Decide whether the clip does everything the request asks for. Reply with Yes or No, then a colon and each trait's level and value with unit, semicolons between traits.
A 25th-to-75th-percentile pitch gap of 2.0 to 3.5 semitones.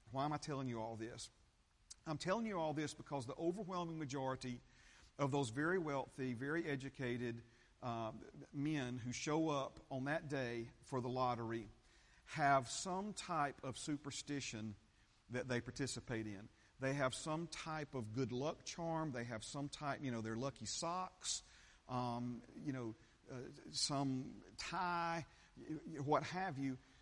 No: average, 4.1 semitones